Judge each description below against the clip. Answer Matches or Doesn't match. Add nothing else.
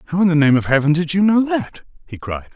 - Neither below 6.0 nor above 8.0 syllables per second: Matches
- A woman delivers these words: Doesn't match